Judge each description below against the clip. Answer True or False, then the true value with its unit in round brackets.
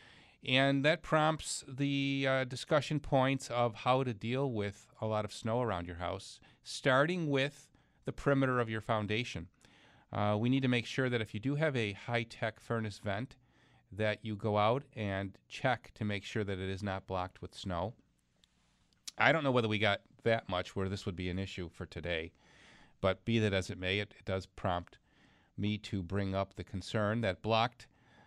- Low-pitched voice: True (110 Hz)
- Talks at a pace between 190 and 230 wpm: True (195 wpm)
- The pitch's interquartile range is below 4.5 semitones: False (4.8 semitones)